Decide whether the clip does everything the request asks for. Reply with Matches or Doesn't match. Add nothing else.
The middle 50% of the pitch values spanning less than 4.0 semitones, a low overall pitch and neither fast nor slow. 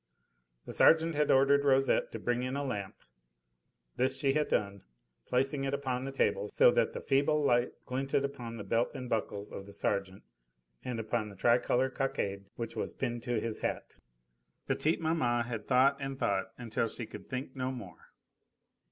Matches